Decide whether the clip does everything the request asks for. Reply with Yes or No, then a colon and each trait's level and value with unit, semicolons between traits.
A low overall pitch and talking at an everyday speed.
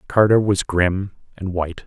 Yes: very low, 95 Hz; average, 160 wpm